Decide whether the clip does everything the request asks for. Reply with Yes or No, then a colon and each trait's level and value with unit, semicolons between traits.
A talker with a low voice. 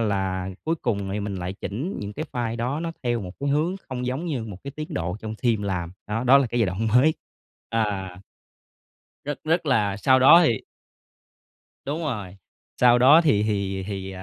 Yes: low, 115 Hz